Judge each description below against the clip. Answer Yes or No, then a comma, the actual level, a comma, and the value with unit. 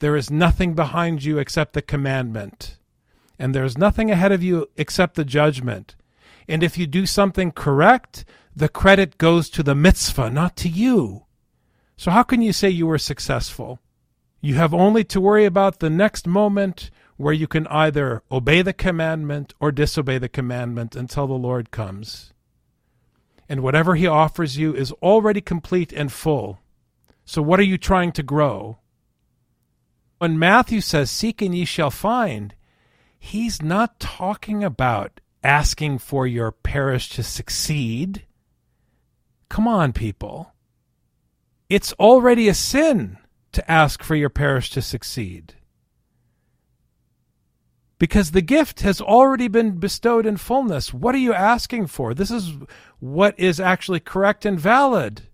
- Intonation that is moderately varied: No, wide, 6.8 semitones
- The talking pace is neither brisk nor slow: Yes, average, 145 wpm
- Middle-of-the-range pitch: Yes, medium, 160 Hz